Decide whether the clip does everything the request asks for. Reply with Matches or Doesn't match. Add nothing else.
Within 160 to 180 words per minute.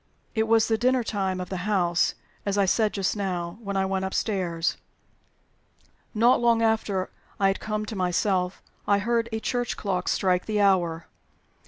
Matches